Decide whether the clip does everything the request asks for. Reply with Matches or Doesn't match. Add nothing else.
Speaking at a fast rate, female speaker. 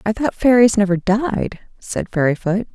Doesn't match